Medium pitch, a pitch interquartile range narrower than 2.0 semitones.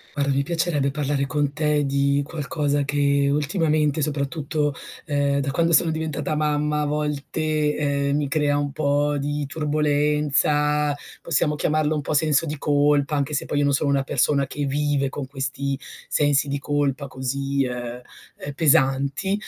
Yes: medium, 145 Hz; narrow, 1.3 semitones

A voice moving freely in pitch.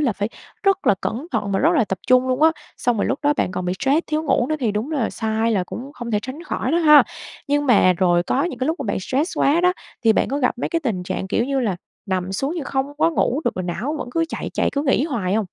Yes: wide, 5.9 semitones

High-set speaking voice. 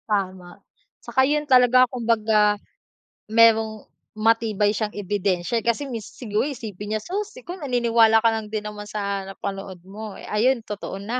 Yes: high, 220 Hz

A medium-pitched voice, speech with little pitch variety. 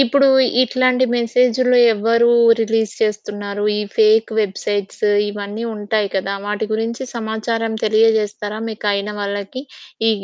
No: high, 220 Hz; narrow, 2.1 semitones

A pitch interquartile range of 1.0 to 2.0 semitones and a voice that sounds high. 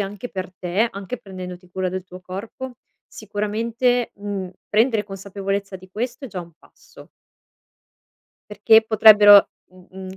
No: average, 2.8 semitones; high, 200 Hz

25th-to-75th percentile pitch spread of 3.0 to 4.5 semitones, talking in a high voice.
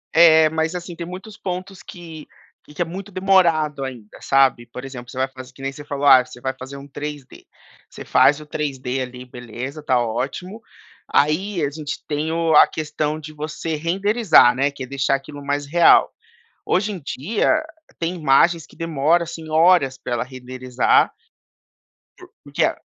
No: average, 4.0 semitones; medium, 150 Hz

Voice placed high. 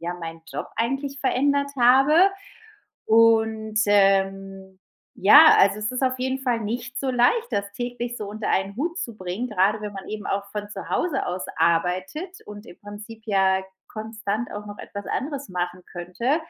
Yes: high, 215 Hz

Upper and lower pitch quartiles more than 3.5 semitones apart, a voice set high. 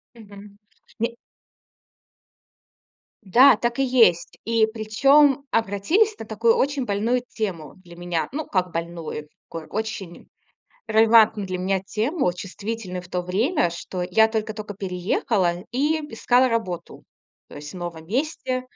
Yes: average, 4.7 semitones; high, 215 Hz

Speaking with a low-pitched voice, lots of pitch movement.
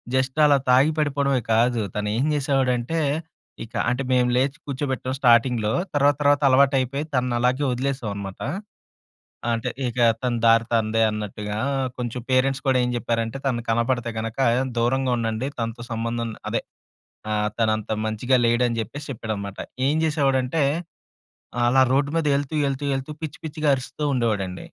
No: low, 125 Hz; average, 3.2 semitones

